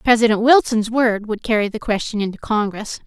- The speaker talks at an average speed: Yes, average, 175 wpm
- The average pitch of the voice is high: Yes, high, 220 Hz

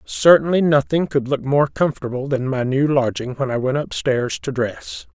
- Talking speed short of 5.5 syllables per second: Yes, 4.8 syllables/s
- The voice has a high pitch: No, low, 135 Hz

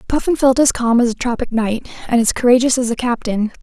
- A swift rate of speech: Yes, fast, 230 wpm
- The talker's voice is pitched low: No, high, 245 Hz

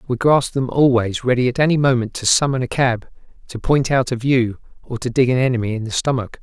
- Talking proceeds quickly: Yes, fast, 235 wpm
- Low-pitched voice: Yes, low, 125 Hz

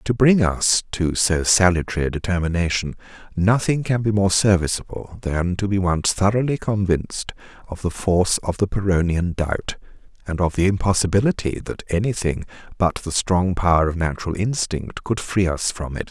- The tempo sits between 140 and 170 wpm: Yes, average, 165 wpm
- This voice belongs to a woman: No, male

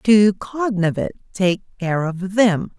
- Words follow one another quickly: No, slow, 110 wpm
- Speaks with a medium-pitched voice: No, high, 195 Hz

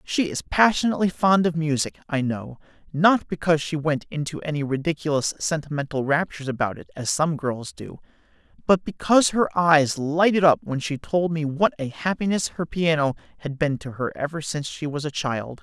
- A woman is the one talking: No, male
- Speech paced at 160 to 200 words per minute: Yes, average, 185 wpm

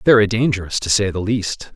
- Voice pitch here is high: No, low, 105 Hz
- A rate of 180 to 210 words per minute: Yes, fast, 205 wpm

